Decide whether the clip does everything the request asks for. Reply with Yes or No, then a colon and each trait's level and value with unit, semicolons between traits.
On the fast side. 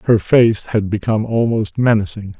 No: average, 150 wpm